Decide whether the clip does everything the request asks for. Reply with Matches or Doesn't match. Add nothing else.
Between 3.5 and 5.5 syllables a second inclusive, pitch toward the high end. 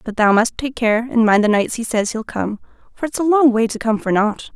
Matches